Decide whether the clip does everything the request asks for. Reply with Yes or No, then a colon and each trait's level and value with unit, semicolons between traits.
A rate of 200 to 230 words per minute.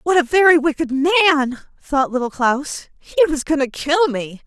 No: average, 190 wpm